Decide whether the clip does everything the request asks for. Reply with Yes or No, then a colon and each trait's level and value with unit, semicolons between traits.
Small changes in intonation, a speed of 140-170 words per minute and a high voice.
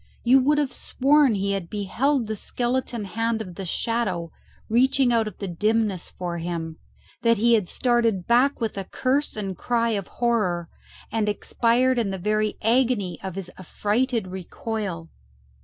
No: average, 4.0 semitones; average, 160 wpm; high, 220 Hz